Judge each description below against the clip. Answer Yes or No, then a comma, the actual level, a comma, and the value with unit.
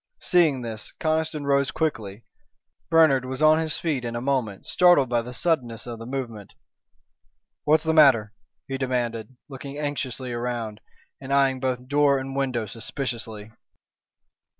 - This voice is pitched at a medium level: No, low, 130 Hz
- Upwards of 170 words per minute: No, average, 145 wpm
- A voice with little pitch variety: No, average, 3.5 semitones